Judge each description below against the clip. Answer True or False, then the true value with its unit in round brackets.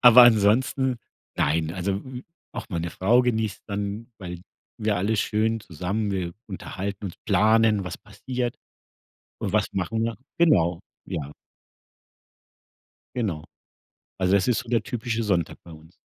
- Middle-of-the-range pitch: False (105 Hz)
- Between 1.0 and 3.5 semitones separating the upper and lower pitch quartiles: False (4.0 semitones)